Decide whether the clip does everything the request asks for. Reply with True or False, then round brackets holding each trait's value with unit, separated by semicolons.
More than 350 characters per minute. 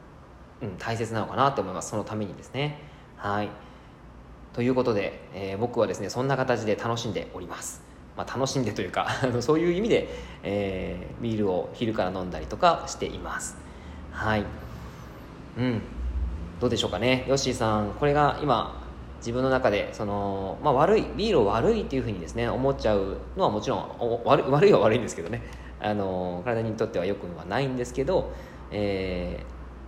True (360 characters per minute)